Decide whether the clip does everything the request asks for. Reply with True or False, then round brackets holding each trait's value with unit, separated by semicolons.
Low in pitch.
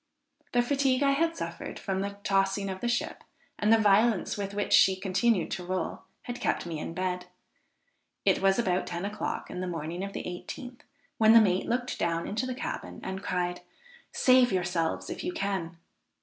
False (195 Hz)